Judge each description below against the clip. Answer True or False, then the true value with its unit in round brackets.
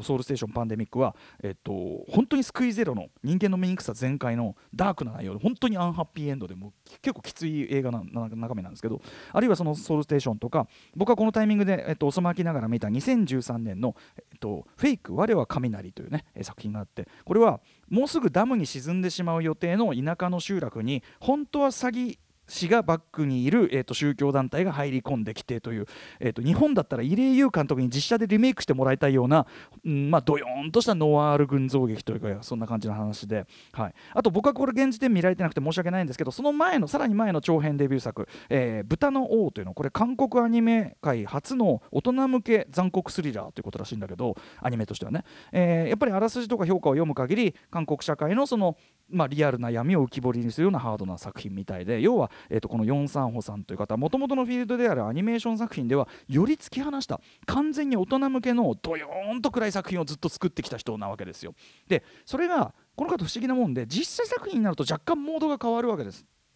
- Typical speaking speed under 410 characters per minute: False (465 characters per minute)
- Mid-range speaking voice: True (165 Hz)